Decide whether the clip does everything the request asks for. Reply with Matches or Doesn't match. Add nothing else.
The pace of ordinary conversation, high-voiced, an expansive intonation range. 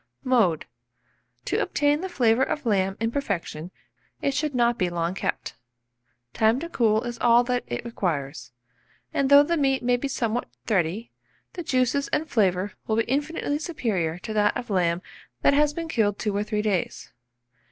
Matches